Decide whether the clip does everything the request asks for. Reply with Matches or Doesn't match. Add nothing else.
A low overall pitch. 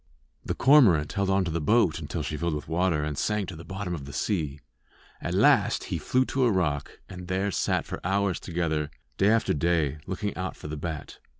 Matches